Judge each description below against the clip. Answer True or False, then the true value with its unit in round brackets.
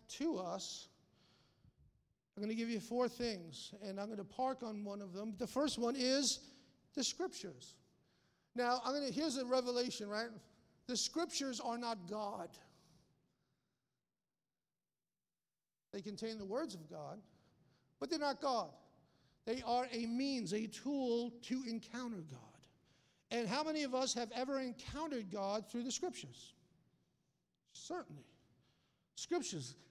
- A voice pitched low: False (240 Hz)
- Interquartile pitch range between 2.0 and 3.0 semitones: False (3.9 semitones)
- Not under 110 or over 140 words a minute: True (135 wpm)